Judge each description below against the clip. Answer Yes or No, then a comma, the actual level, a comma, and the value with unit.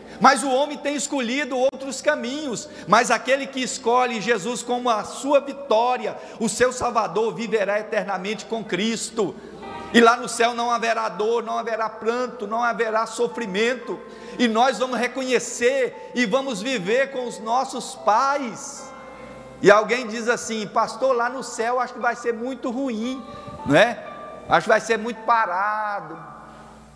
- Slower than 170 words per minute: Yes, average, 155 wpm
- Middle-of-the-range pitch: No, high, 235 Hz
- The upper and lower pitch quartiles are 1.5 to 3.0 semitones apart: Yes, average, 2.7 semitones